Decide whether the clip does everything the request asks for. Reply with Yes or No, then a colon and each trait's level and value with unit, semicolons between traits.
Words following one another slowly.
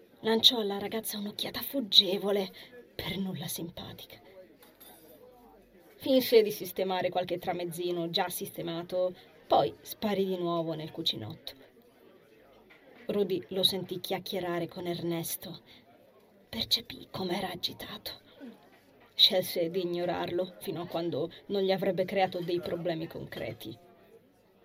Yes: slow, 105 wpm